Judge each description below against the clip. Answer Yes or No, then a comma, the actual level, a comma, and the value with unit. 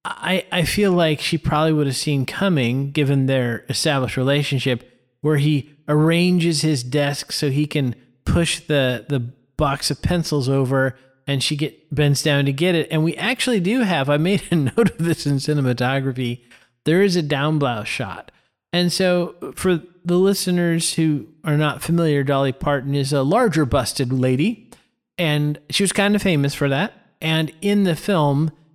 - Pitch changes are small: No, average, 3.7 semitones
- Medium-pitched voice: Yes, medium, 150 Hz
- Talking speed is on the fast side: No, average, 175 wpm